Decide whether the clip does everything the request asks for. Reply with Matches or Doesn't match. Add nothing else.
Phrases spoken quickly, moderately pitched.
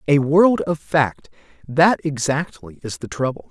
Doesn't match